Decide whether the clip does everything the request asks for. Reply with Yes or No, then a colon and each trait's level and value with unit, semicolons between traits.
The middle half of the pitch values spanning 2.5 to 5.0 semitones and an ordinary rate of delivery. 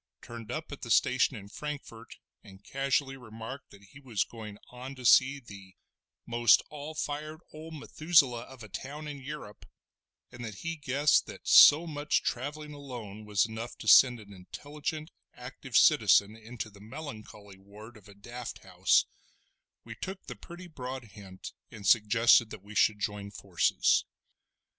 No: wide, 5.4 semitones; average, 160 wpm